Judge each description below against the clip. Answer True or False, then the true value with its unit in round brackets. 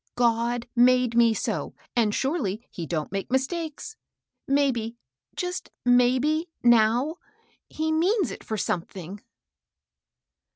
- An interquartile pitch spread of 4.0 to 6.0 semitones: True (5.1 semitones)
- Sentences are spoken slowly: True (115 wpm)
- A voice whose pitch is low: False (245 Hz)